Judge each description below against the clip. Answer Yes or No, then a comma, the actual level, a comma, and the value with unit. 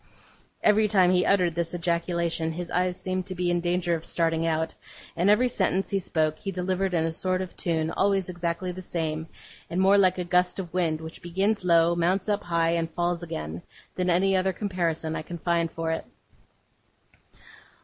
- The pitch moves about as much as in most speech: No, narrow, 2.0 semitones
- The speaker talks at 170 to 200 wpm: Yes, average, 190 wpm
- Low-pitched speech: No, medium, 175 Hz